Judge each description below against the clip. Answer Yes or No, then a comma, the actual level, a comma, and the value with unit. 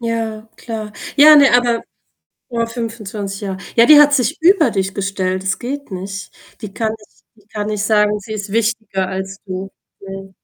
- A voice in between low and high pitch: No, high, 215 Hz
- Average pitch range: Yes, average, 3.1 semitones